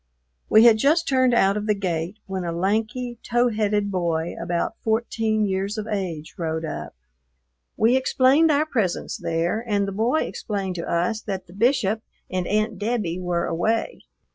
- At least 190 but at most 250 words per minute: No, average, 165 wpm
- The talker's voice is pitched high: Yes, high, 210 Hz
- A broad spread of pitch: No, average, 4.2 semitones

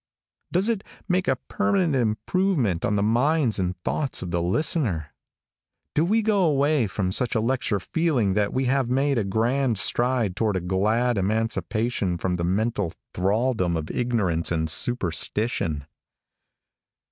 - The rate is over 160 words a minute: No, average, 145 wpm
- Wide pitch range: Yes, wide, 6.5 semitones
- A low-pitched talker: Yes, low, 115 Hz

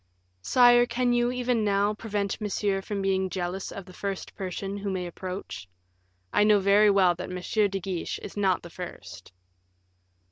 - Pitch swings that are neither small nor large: No, narrow, 2.3 semitones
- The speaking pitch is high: Yes, high, 195 Hz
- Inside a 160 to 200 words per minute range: Yes, average, 170 wpm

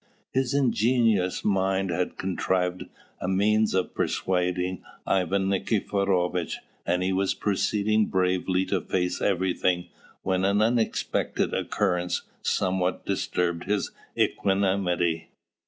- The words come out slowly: Yes, slow, 105 wpm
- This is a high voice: No, very low, 95 Hz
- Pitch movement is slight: Yes, narrow, 1.9 semitones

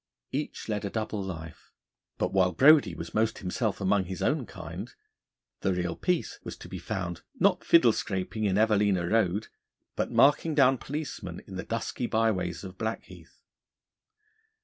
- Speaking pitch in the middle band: No, low, 105 Hz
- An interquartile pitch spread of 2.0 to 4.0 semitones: Yes, average, 3.6 semitones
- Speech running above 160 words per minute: No, average, 155 wpm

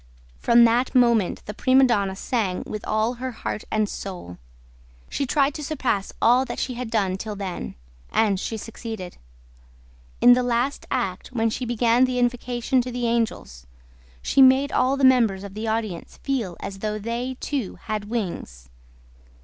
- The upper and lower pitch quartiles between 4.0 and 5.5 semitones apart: No, average, 3.6 semitones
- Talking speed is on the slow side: No, average, 165 wpm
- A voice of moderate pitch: No, high, 230 Hz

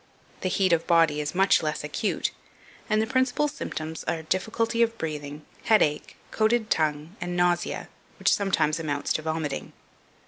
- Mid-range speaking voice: Yes, medium, 170 Hz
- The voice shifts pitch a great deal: Yes, wide, 5.9 semitones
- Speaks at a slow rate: No, average, 150 wpm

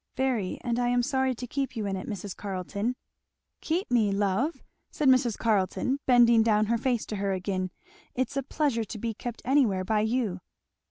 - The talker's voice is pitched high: Yes, high, 230 Hz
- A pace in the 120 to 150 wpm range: No, average, 195 wpm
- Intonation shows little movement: No, average, 4.1 semitones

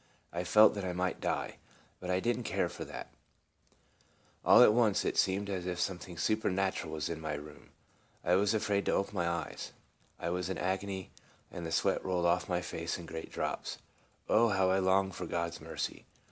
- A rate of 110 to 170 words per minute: No, fast, 205 wpm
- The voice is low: Yes, very low, 95 Hz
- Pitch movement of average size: No, narrow, 2.3 semitones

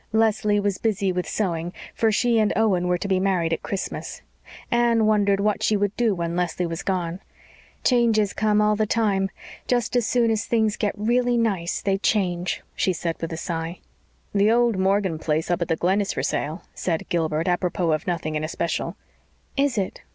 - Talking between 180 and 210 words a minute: Yes, average, 195 wpm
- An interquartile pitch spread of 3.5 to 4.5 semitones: Yes, average, 3.8 semitones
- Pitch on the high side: Yes, high, 195 Hz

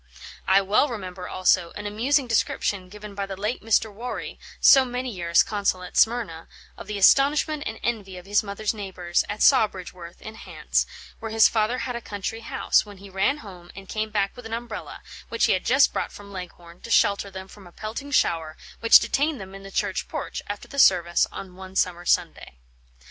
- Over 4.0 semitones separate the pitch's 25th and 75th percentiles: No, average, 3.2 semitones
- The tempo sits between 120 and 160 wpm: No, average, 200 wpm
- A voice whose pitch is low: No, high, 205 Hz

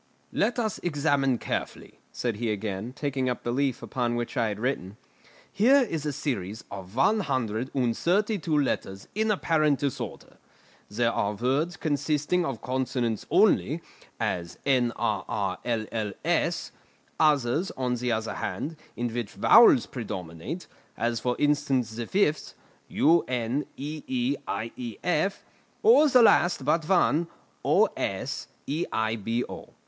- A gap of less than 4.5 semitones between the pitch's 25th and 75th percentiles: No, average, 5.3 semitones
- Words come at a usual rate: No, slow, 120 wpm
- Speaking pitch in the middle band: No, low, 130 Hz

